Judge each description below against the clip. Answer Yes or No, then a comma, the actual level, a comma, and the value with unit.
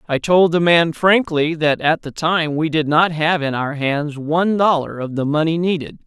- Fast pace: Yes, fast, 215 wpm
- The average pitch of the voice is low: No, medium, 160 Hz